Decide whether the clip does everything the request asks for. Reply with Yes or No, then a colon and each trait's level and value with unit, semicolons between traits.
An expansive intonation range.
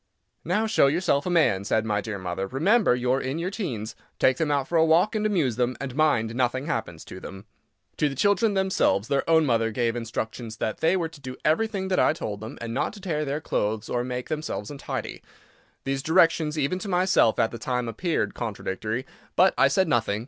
Yes: wide, 6.7 semitones